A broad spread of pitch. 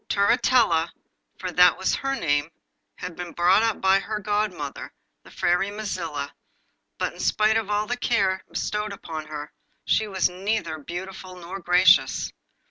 No: average, 3.5 semitones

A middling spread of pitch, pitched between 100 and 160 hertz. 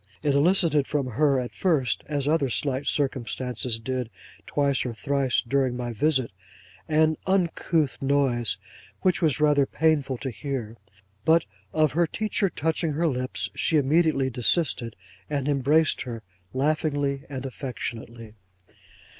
Yes: average, 3.3 semitones; medium, 140 Hz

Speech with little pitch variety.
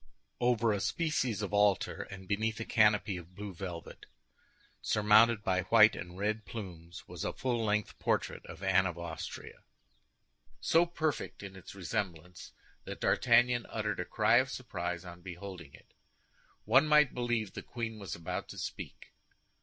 No: average, 4.1 semitones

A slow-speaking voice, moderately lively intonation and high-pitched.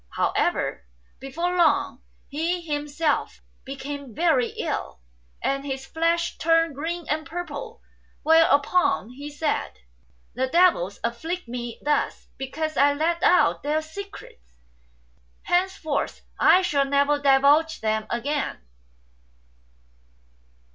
Yes: slow, 105 wpm; average, 3.5 semitones; very high, 295 Hz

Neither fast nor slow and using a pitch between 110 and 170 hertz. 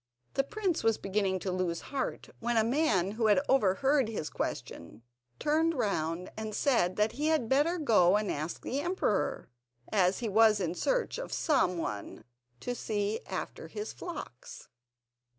No: average, 160 wpm; high, 220 Hz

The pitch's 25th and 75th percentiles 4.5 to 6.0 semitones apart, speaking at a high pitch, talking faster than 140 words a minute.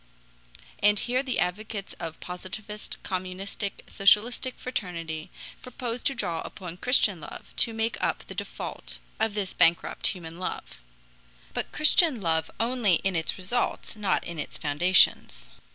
No: average, 4.8 semitones; high, 195 Hz; slow, 135 wpm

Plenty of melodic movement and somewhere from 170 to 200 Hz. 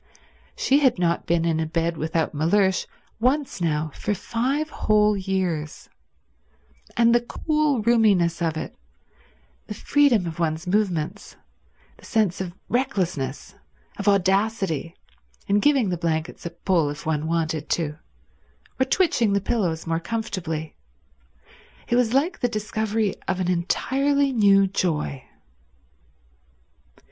Yes: wide, 5.7 semitones; high, 190 Hz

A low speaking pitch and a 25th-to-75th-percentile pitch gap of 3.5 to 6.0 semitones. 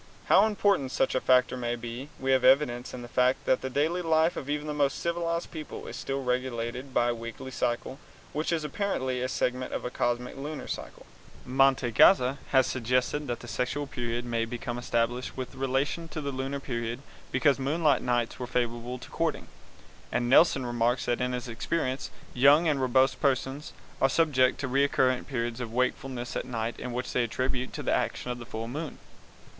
No: low, 130 Hz; narrow, 2.4 semitones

